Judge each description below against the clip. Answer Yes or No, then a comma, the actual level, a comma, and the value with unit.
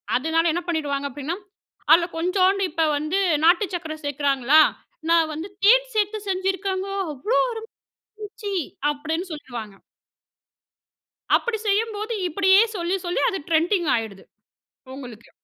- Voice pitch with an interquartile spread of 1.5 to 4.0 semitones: No, average, 4.9 semitones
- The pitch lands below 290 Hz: No, very high, 340 Hz